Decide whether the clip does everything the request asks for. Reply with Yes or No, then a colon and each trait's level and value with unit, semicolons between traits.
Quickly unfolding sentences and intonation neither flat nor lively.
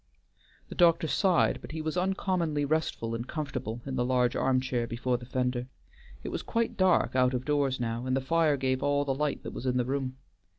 Yes: fast, 215 wpm; average, 3.8 semitones